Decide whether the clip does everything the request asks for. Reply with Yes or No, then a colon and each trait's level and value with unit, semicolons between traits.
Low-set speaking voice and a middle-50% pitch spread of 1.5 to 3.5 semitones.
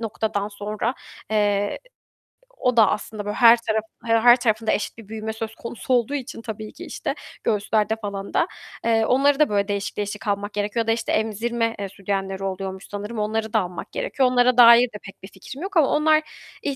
No: high, 220 Hz; narrow, 2.6 semitones